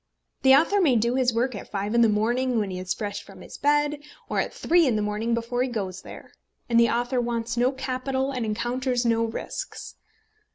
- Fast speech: Yes, fast, 215 wpm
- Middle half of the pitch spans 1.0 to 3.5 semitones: Yes, average, 2.7 semitones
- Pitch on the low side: No, high, 240 Hz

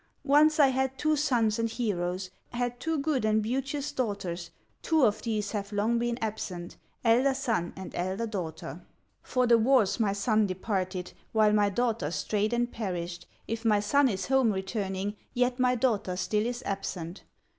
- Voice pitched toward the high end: Yes, high, 220 Hz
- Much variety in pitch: No, average, 4.1 semitones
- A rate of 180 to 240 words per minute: No, average, 165 wpm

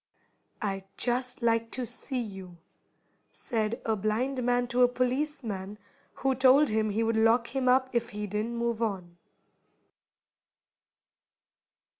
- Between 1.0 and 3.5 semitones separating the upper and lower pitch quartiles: Yes, average, 2.9 semitones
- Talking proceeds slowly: Yes, slow, 130 wpm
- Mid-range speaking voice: No, high, 235 Hz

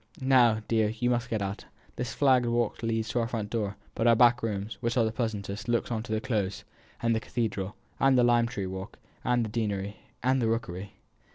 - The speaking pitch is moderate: No, low, 115 Hz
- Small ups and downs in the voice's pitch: Yes, narrow, 2.3 semitones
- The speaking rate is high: Yes, fast, 215 wpm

